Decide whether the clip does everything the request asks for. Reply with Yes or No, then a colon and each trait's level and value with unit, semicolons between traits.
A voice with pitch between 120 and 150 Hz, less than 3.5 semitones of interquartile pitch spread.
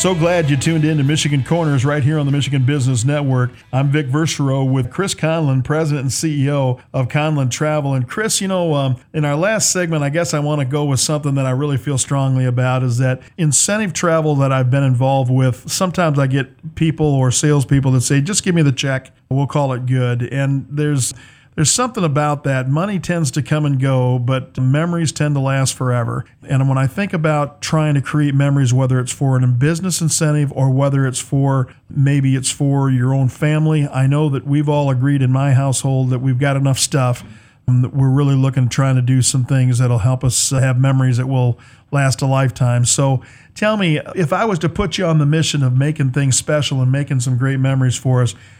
Yes: medium, 140 Hz; narrow, 2.5 semitones